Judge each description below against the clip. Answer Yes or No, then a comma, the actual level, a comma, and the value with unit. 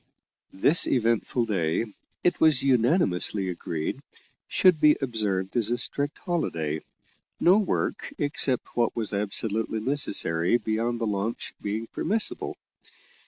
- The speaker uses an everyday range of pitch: No, wide, 6.1 semitones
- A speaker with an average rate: No, slow, 120 wpm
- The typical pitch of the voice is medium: No, low, 115 Hz